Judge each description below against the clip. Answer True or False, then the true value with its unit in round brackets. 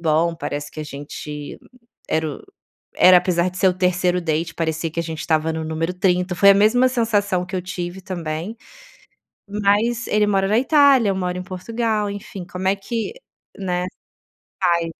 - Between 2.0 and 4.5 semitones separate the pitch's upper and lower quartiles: True (3.4 semitones)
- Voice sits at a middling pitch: True (180 Hz)